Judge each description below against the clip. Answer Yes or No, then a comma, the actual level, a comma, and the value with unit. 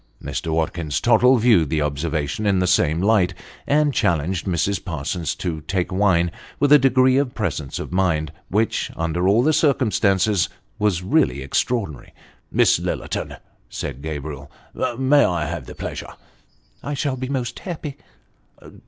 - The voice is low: Yes, very low, 95 Hz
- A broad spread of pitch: Yes, wide, 7.6 semitones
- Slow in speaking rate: No, average, 160 wpm